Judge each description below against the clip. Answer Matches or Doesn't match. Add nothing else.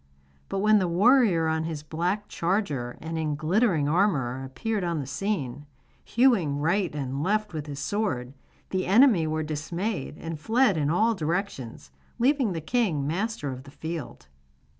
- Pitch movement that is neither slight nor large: Doesn't match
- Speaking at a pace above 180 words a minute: Doesn't match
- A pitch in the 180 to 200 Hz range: Doesn't match